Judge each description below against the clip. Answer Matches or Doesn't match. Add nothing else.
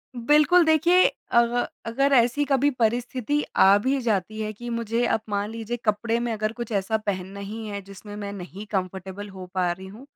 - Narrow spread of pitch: Doesn't match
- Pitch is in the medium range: Doesn't match